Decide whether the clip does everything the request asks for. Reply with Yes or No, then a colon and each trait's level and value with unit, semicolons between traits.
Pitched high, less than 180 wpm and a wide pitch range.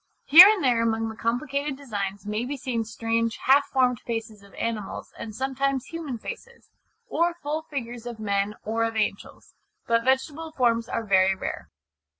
No: high, 235 Hz; average, 165 wpm; average, 3.9 semitones